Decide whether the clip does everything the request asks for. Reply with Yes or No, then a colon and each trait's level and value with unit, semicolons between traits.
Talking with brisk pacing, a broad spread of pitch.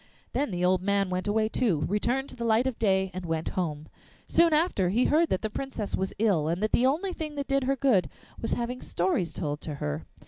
Yes: fast, 235 wpm; wide, 6.4 semitones